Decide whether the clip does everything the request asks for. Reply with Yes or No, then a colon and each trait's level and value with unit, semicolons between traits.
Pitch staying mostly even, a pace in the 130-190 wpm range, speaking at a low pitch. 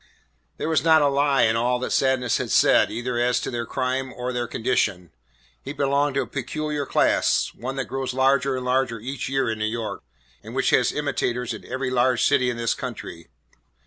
No: narrow, 2.2 semitones; fast, 205 wpm; low, 130 Hz